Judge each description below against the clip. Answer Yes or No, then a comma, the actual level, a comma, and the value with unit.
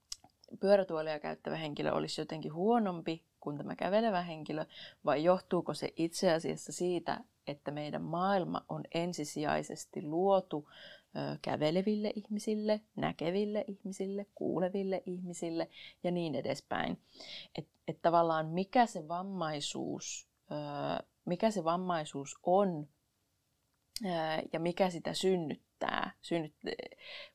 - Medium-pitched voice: Yes, medium, 175 Hz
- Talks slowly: No, average, 110 wpm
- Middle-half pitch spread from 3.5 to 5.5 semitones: Yes, average, 3.8 semitones